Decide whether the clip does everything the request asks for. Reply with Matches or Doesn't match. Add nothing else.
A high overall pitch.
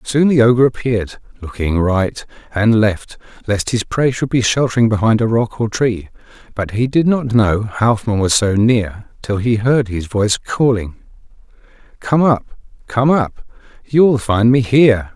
Doesn't match